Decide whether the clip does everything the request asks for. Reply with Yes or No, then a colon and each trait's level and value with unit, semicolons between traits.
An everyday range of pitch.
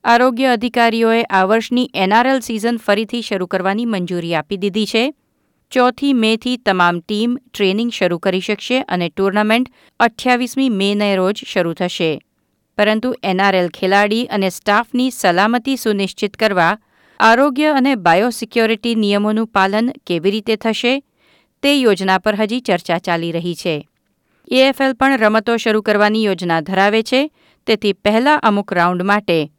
Yes: average, 4.1 semitones